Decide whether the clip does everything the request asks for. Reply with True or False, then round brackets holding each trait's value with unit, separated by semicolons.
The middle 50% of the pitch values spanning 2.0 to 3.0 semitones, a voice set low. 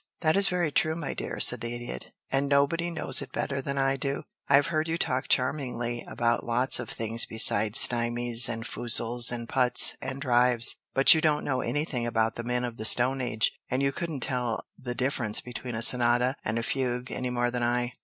True (2.6 semitones; 125 Hz)